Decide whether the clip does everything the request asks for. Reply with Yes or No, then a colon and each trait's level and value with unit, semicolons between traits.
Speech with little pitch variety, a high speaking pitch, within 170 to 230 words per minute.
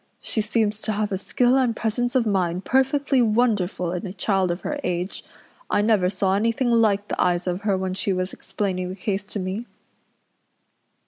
No: average, 3.7 semitones; high, 205 Hz; average, 190 wpm